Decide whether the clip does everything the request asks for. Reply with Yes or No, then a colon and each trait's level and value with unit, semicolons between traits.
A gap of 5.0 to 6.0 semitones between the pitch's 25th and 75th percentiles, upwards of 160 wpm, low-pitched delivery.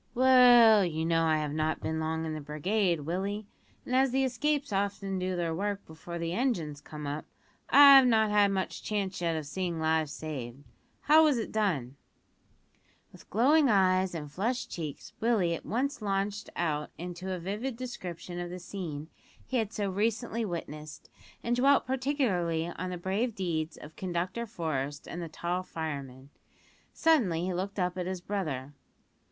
No: wide, 5.5 semitones; average, 170 wpm; medium, 185 Hz